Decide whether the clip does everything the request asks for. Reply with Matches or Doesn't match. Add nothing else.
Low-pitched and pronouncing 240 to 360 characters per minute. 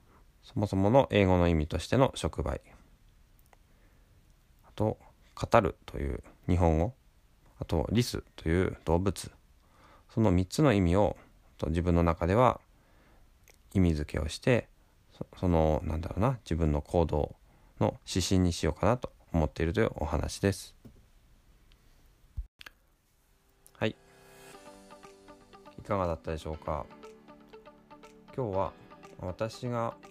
Doesn't match